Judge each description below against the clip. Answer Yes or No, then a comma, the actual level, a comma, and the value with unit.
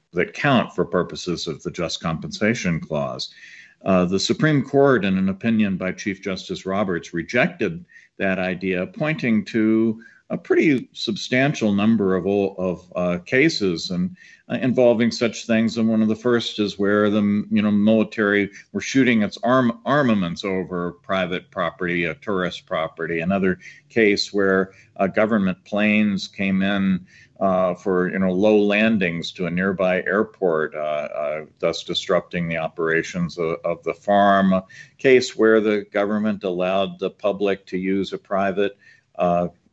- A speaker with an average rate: Yes, average, 155 wpm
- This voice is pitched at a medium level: No, low, 100 Hz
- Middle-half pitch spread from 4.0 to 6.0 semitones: No, average, 3.1 semitones